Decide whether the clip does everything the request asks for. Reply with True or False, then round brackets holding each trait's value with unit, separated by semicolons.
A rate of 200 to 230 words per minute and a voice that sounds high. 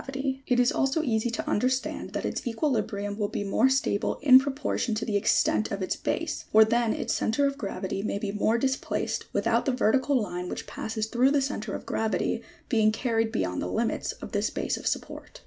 True (205 wpm; 225 Hz)